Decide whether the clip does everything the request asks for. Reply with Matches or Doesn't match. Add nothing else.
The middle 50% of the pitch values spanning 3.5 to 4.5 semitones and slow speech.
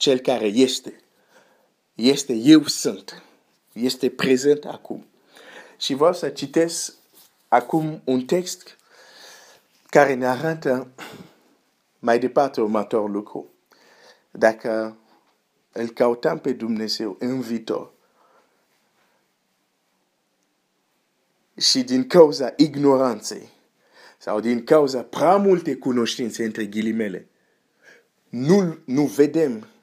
Doesn't match